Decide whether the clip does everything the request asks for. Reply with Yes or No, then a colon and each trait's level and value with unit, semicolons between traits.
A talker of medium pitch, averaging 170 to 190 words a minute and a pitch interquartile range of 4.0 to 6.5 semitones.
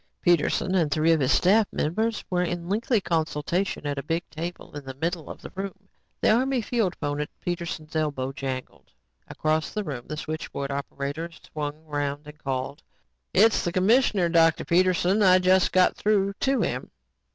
Yes: medium, 170 Hz; average, 175 wpm; average, 4.4 semitones